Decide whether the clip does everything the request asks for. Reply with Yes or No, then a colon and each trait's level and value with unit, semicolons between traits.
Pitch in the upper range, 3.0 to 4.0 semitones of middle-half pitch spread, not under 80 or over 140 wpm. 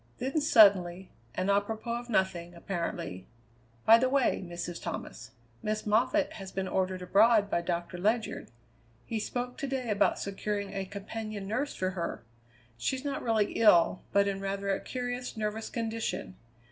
No: high, 205 Hz; average, 3.6 semitones; average, 155 wpm